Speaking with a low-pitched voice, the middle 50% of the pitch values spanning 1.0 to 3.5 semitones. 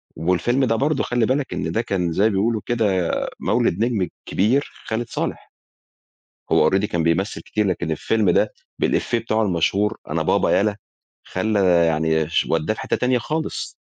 No: low, 105 Hz; average, 4.7 semitones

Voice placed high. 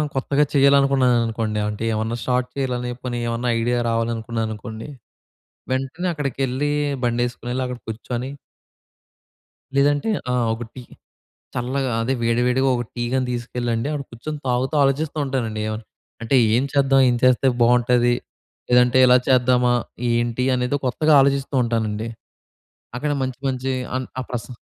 No: low, 125 Hz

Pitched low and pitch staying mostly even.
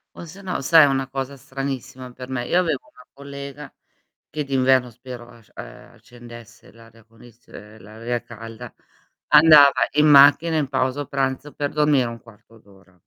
No: low, 130 Hz; average, 3.3 semitones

